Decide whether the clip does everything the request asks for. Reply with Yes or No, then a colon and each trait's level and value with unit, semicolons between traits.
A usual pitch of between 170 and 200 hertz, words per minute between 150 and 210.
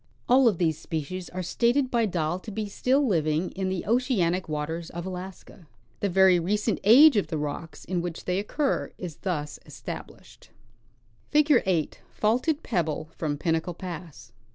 Yes: medium, 185 Hz; average, 165 wpm